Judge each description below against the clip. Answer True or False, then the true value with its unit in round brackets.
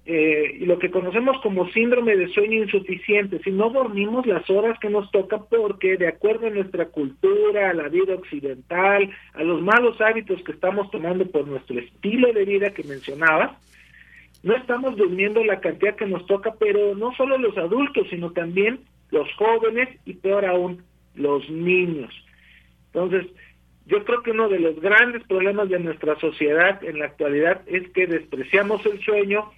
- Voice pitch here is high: True (195 Hz)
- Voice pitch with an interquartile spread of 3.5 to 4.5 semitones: True (3.8 semitones)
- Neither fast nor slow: True (170 wpm)